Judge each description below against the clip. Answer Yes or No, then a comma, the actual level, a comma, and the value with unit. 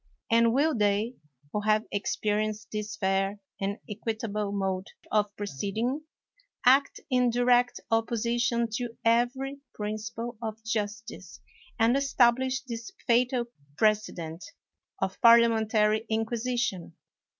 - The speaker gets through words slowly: Yes, slow, 105 wpm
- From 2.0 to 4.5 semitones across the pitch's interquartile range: Yes, narrow, 2.4 semitones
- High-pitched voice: Yes, high, 225 Hz